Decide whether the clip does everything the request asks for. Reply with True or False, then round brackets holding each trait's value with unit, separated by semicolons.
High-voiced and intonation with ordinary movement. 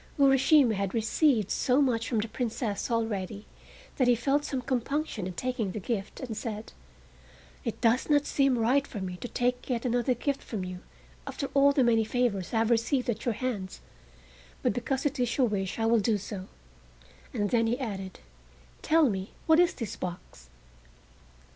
True (235 Hz; 3.8 semitones)